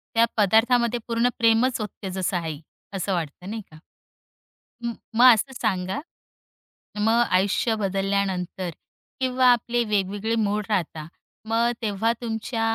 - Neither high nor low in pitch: No, high, 215 Hz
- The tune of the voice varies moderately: Yes, average, 3.3 semitones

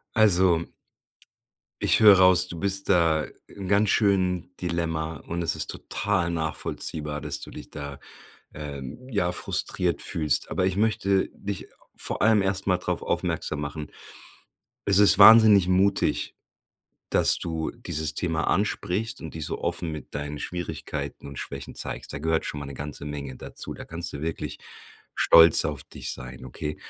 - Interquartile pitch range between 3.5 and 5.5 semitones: Yes, average, 4.4 semitones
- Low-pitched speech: Yes, very low, 85 Hz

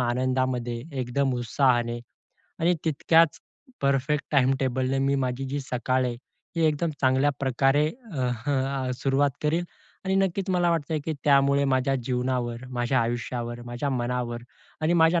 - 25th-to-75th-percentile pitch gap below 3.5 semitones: Yes, average, 2.8 semitones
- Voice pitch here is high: No, low, 130 Hz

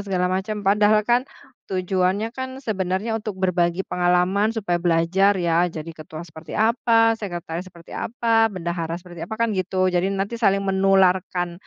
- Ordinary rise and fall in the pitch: Yes, average, 3.3 semitones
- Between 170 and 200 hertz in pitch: Yes, high, 190 Hz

